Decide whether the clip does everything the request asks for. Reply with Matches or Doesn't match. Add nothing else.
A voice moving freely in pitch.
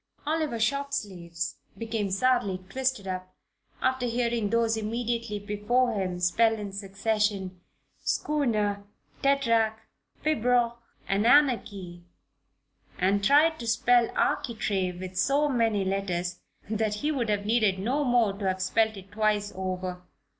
Doesn't match